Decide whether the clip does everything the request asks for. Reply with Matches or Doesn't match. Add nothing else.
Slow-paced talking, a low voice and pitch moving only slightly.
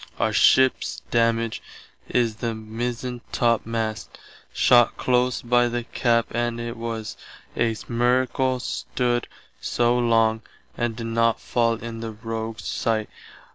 Matches